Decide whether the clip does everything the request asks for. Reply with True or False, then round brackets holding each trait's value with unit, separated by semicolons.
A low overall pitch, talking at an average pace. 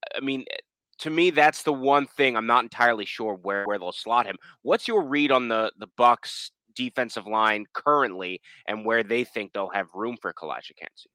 True (115 Hz; 195 wpm)